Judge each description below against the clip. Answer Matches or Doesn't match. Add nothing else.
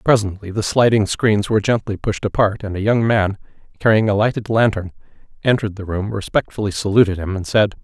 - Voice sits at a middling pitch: Doesn't match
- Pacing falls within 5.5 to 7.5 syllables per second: Matches